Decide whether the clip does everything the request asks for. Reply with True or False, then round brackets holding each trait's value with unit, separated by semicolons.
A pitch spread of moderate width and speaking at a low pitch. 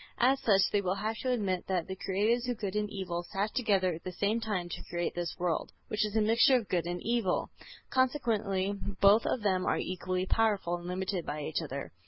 False (3.4 semitones; 195 Hz)